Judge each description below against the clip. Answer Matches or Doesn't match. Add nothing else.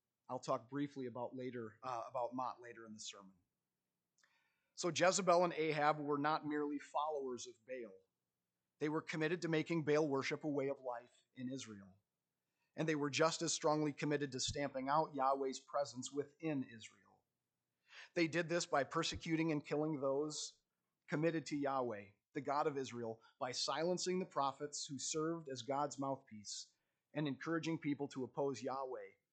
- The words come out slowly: Doesn't match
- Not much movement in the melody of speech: Doesn't match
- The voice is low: Doesn't match